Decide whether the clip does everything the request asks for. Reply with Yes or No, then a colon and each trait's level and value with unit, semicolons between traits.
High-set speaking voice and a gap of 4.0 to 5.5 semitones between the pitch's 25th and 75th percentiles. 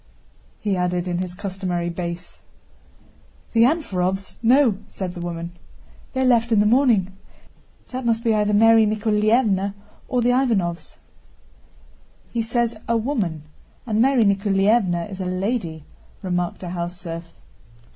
Yes: high, 200 Hz; average, 4.5 semitones